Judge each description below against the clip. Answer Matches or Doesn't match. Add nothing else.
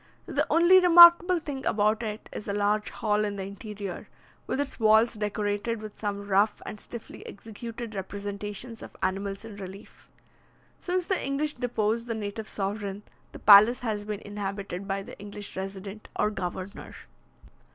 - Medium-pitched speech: Doesn't match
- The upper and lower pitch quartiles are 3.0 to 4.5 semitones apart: Doesn't match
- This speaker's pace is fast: Doesn't match